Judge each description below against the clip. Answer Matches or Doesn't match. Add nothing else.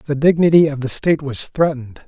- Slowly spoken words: Doesn't match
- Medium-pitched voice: Matches